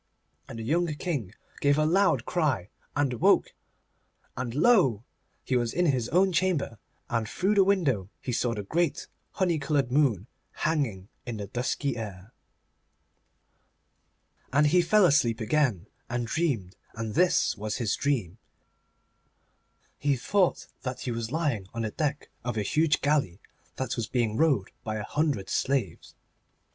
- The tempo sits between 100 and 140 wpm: No, average, 150 wpm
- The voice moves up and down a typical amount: No, wide, 5.8 semitones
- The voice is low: Yes, low, 130 Hz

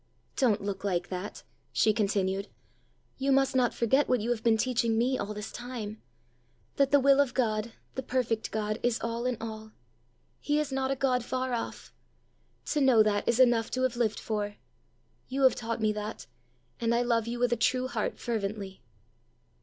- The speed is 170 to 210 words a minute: Yes, average, 185 wpm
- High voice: Yes, high, 235 Hz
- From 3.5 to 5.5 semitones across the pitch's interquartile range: No, average, 3.1 semitones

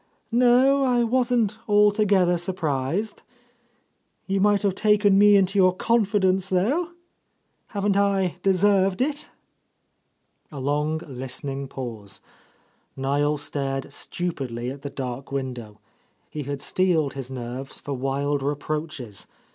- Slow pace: Yes, slow, 125 wpm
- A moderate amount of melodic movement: No, wide, 7.0 semitones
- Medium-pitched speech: Yes, medium, 175 Hz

